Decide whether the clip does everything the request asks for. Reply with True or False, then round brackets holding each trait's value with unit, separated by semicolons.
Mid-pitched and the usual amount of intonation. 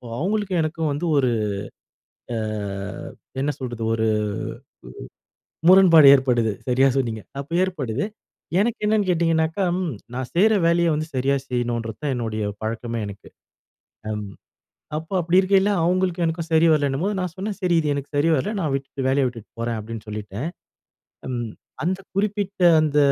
False (150 Hz; 6.7 semitones)